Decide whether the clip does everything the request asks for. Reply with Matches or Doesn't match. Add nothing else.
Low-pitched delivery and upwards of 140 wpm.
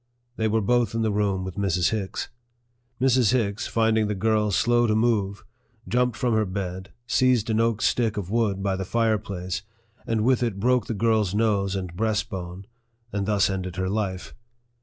Matches